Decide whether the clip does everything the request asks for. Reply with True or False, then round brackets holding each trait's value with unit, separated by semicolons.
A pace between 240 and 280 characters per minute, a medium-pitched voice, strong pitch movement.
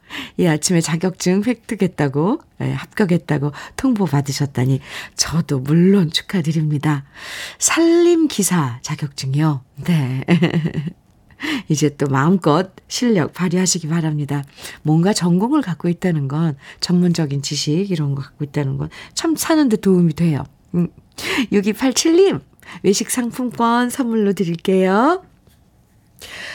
True (245 characters per minute; 175 Hz; 6.0 semitones)